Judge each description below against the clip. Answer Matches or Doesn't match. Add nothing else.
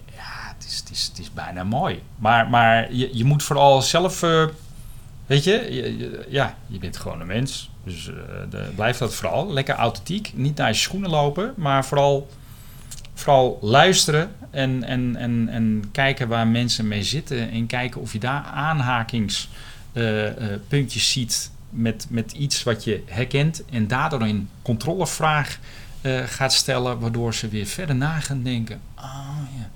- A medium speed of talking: Matches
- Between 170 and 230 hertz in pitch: Doesn't match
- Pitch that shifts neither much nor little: Matches